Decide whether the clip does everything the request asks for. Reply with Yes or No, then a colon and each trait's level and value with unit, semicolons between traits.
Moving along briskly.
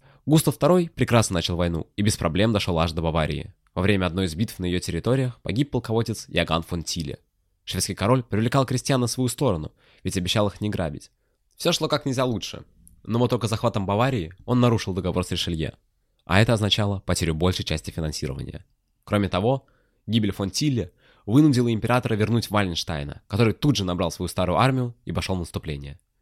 Yes: fast, 185 wpm